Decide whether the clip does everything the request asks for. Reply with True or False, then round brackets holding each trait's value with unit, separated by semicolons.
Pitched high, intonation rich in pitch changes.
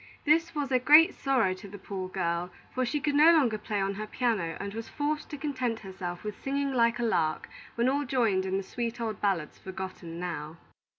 True (220 Hz; 6.3 semitones)